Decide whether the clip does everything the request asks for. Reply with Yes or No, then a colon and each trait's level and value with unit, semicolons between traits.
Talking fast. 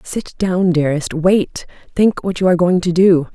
No: average, 180 wpm